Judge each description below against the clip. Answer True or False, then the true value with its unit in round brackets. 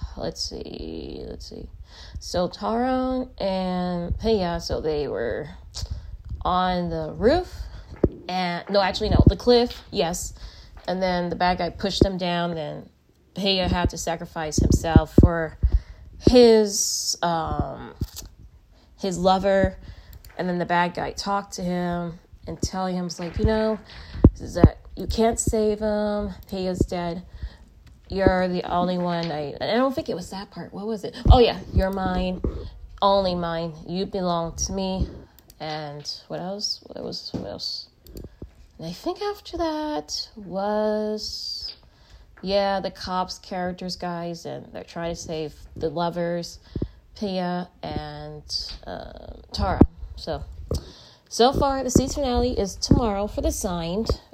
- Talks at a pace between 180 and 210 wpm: False (145 wpm)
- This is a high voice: False (180 Hz)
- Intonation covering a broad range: False (3.6 semitones)